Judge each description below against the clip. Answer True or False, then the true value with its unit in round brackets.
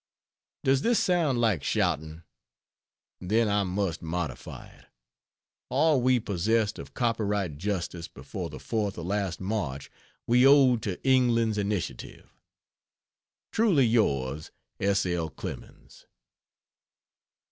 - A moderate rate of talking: False (110 wpm)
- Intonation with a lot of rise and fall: True (5.7 semitones)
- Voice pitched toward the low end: True (105 Hz)